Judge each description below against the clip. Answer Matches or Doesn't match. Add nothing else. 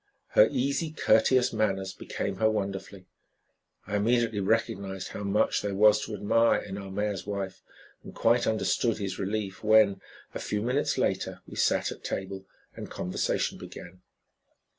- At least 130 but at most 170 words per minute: Matches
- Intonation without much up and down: Matches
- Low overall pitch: Matches